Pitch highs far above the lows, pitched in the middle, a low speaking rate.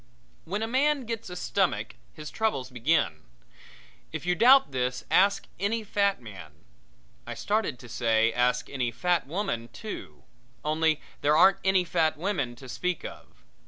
No: wide, 8.2 semitones; medium, 160 Hz; average, 155 wpm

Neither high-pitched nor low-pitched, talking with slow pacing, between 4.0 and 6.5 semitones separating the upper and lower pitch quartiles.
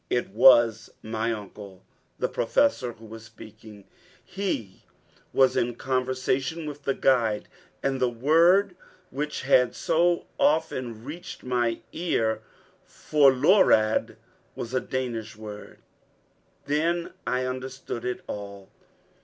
No: low, 125 Hz; slow, 110 wpm; average, 4.6 semitones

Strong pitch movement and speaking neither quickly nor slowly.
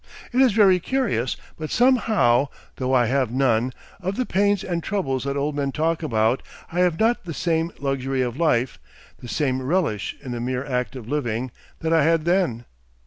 Yes: wide, 5.9 semitones; average, 190 wpm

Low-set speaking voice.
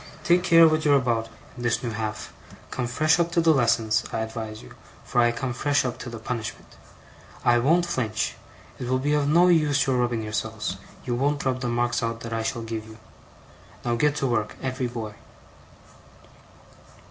Yes: low, 120 Hz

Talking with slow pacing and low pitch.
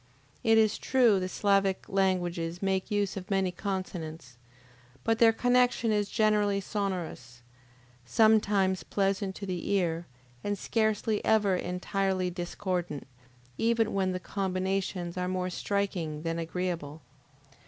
No: slow, 120 wpm; high, 190 Hz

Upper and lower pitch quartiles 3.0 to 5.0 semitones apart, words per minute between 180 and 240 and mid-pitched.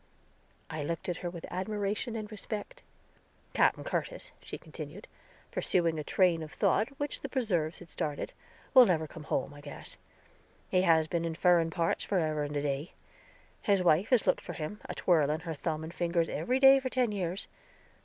Yes: average, 4.7 semitones; average, 185 wpm; medium, 175 Hz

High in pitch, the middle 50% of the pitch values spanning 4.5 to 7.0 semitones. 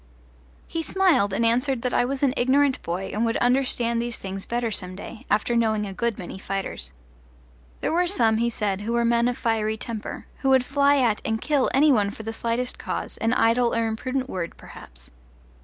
No: high, 235 Hz; average, 3.1 semitones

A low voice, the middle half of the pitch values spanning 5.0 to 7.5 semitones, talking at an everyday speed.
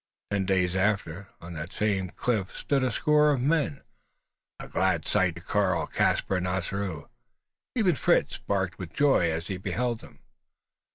Yes: very low, 95 Hz; wide, 5.4 semitones; average, 160 wpm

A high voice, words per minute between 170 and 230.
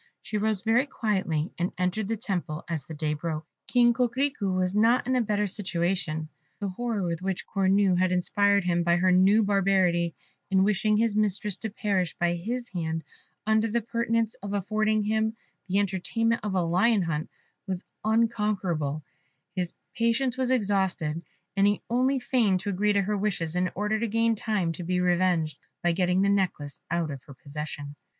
Yes: high, 195 Hz; average, 180 wpm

